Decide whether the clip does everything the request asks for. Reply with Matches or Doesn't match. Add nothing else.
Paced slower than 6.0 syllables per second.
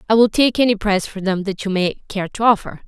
Doesn't match